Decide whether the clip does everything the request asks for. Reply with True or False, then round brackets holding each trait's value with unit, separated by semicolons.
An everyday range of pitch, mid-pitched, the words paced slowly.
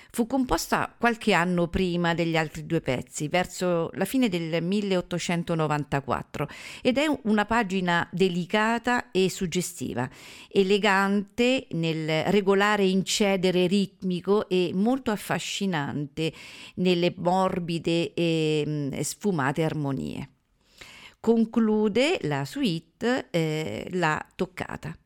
True (4.1 semitones; 180 Hz; 95 wpm)